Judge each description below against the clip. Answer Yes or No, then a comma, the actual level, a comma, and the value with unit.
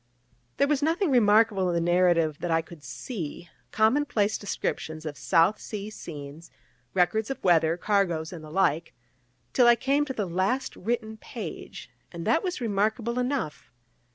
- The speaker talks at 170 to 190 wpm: No, average, 160 wpm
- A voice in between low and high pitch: No, high, 200 Hz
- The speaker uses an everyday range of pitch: No, wide, 6.0 semitones